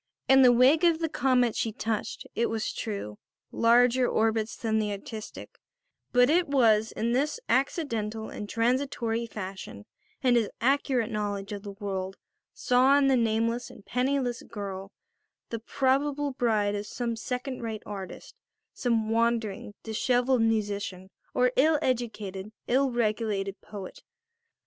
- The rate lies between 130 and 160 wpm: Yes, average, 140 wpm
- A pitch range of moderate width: Yes, average, 3.3 semitones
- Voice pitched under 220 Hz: No, high, 230 Hz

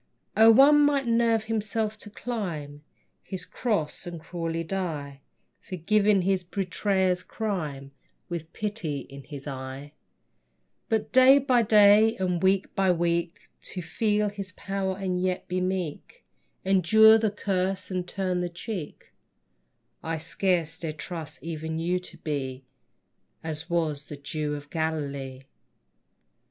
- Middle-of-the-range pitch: Yes, medium, 180 Hz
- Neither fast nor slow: No, slow, 130 wpm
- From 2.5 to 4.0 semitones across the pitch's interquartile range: No, average, 4.6 semitones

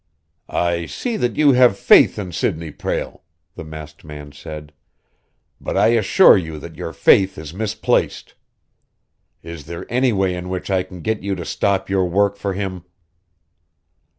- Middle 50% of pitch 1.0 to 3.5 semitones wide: No, average, 3.9 semitones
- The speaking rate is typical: Yes, average, 160 wpm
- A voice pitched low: Yes, very low, 90 Hz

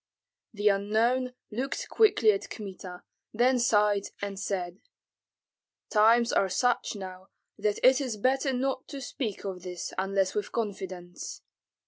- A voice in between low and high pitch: No, high, 210 Hz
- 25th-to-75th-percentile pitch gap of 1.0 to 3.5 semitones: No, average, 4.3 semitones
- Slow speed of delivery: Yes, slow, 130 wpm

